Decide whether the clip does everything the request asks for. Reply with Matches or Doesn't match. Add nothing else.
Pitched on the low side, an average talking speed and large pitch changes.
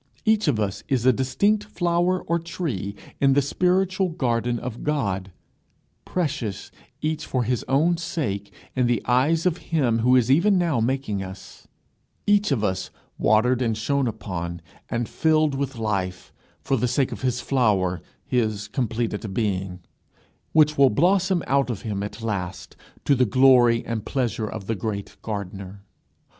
Matches